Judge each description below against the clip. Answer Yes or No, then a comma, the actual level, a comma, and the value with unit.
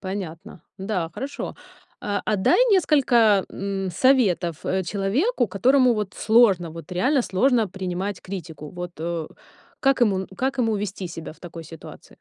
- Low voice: No, high, 195 Hz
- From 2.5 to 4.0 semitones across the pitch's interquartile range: No, average, 4.9 semitones